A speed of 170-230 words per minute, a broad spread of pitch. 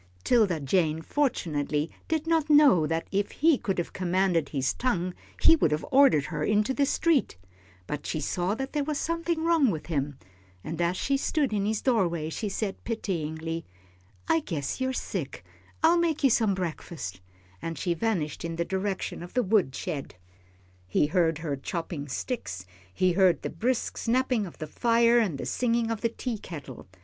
Yes: average, 180 wpm; wide, 7.7 semitones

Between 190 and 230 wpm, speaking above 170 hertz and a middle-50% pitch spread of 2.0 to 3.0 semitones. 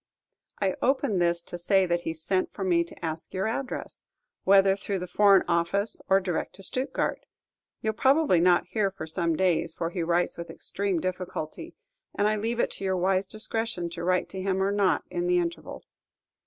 Yes: average, 195 wpm; medium, 185 Hz; narrow, 2.6 semitones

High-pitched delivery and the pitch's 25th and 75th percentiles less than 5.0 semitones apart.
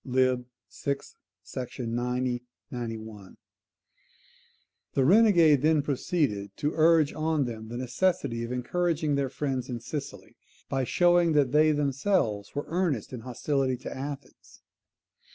No: low, 135 Hz; average, 4.1 semitones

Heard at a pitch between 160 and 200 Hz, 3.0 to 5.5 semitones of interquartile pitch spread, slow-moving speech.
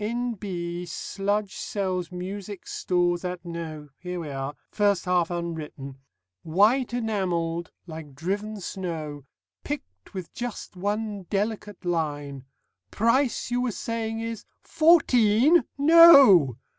Yes: high, 190 Hz; average, 4.8 semitones; slow, 115 wpm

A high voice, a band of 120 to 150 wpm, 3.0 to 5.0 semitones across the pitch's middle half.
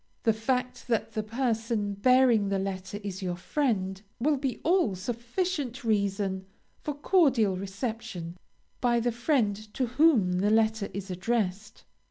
Yes: high, 220 Hz; average, 140 wpm; average, 4.3 semitones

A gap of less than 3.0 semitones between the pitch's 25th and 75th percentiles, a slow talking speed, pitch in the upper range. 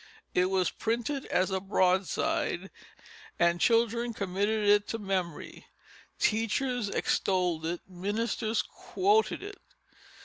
No: average, 3.7 semitones; slow, 105 wpm; high, 205 Hz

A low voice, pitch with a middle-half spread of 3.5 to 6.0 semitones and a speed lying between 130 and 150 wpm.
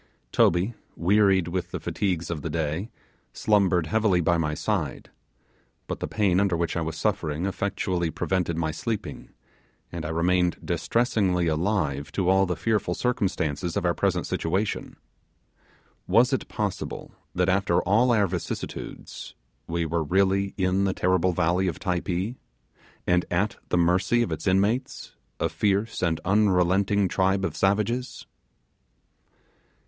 No: very low, 90 Hz; narrow, 2.6 semitones; average, 140 wpm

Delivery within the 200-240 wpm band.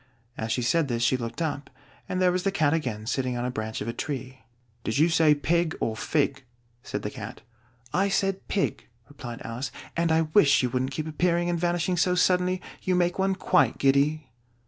Yes: fast, 205 wpm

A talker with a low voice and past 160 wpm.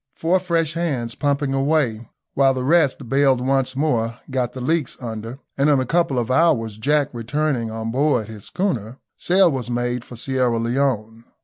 Yes: low, 130 Hz; average, 175 wpm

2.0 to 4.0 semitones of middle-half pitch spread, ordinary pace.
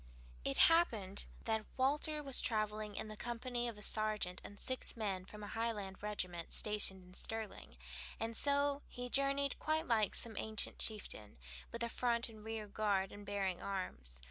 Yes: average, 3.1 semitones; average, 170 wpm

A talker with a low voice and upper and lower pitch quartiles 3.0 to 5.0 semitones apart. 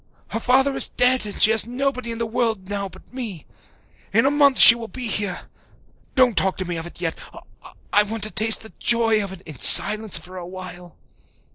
No: high, 220 Hz; average, 4.3 semitones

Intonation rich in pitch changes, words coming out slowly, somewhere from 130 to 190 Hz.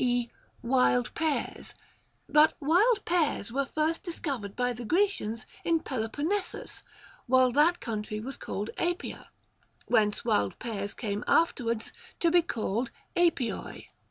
No: wide, 6.7 semitones; slow, 130 wpm; very high, 255 Hz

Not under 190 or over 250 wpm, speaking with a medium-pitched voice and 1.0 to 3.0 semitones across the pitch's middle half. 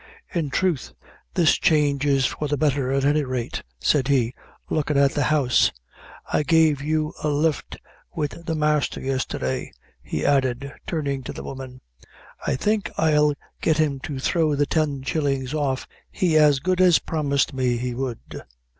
No: average, 165 wpm; medium, 145 Hz; narrow, 2.5 semitones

